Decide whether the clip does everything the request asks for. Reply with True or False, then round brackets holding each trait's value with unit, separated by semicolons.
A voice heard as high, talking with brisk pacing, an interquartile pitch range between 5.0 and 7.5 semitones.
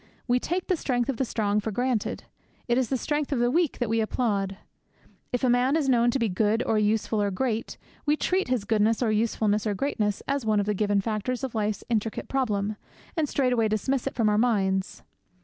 False (230 Hz; 220 wpm; 3.4 semitones)